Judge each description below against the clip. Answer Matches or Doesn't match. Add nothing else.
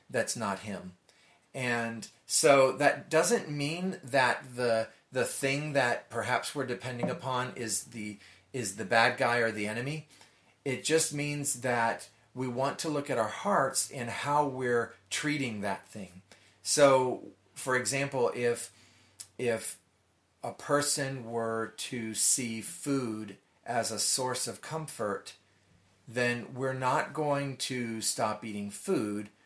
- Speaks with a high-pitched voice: Doesn't match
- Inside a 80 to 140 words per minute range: Matches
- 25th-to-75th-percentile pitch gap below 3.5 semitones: Doesn't match